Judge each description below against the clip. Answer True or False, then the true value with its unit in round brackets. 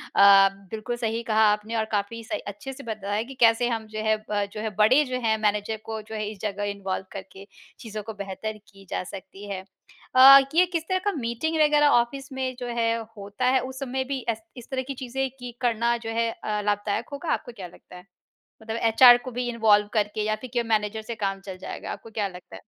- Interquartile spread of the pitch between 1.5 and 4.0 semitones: True (3.3 semitones)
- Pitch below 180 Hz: False (220 Hz)